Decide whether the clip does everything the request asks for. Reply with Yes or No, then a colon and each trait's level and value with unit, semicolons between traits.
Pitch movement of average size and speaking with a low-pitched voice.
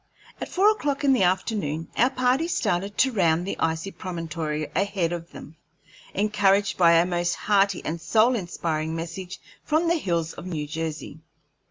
No: average, 4.5 semitones; medium, 180 Hz